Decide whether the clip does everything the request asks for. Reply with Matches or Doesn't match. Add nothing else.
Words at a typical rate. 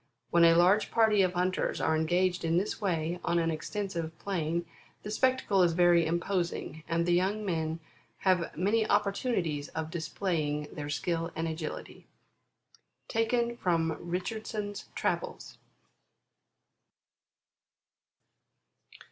Doesn't match